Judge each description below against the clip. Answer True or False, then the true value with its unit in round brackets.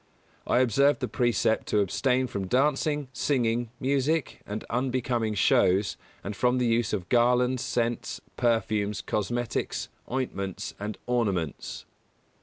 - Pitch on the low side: True (120 Hz)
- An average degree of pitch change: True (3.3 semitones)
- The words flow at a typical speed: False (120 wpm)